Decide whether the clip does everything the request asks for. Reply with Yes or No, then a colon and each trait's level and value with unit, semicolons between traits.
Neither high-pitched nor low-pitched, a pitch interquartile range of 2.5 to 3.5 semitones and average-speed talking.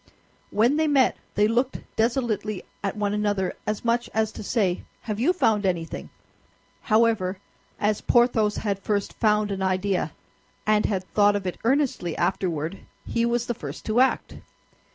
No: high, 210 Hz; average, 3.1 semitones; average, 155 wpm